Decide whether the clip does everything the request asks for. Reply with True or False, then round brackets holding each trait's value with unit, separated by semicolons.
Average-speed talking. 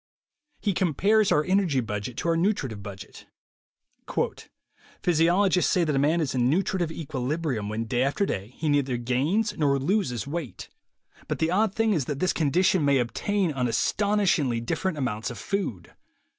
True (165 wpm)